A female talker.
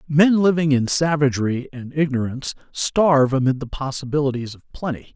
No: male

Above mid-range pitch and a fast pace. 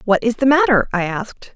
Yes: high, 235 Hz; fast, 230 wpm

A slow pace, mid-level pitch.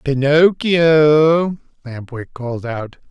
Yes: slow, 95 wpm; medium, 145 Hz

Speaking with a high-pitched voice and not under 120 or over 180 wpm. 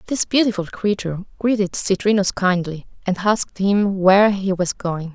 Yes: high, 195 Hz; average, 150 wpm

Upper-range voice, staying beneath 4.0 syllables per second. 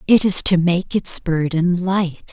No: medium, 175 Hz; 3.7 syllables/s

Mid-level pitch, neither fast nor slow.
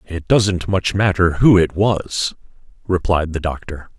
No: very low, 90 Hz; average, 150 wpm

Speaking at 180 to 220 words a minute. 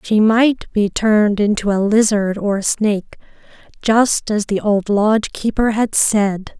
No: average, 165 wpm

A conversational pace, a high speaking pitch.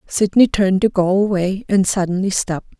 Yes: average, 150 wpm; high, 195 Hz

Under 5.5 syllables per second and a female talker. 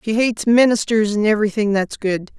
No: 5.8 syllables/s; female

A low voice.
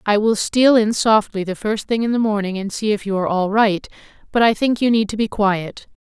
No: high, 210 Hz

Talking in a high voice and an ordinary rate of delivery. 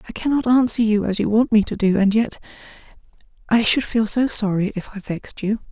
No: high, 215 Hz; fast, 220 wpm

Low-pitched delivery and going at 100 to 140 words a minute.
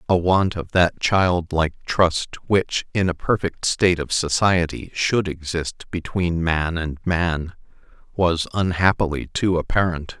Yes: very low, 85 Hz; slow, 135 wpm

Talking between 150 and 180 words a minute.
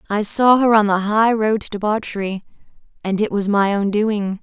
No: fast, 205 wpm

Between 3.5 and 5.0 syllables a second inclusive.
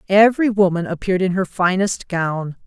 No: 5.4 syllables/s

